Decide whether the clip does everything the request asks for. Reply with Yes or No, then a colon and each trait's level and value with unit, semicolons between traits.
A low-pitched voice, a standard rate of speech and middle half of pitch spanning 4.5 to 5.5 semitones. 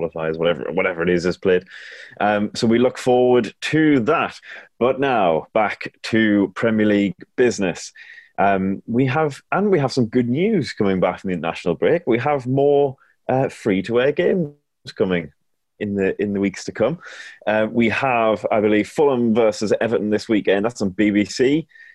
Yes: low, 110 Hz; average, 170 wpm; average, 5.2 semitones